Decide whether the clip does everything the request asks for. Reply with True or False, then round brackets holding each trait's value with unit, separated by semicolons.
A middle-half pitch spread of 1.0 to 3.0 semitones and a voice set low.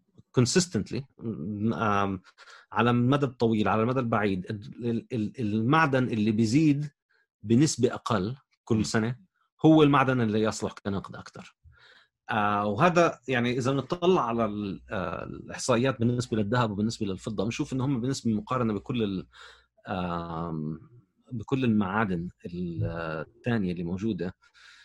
False (3.8 semitones; 115 Hz)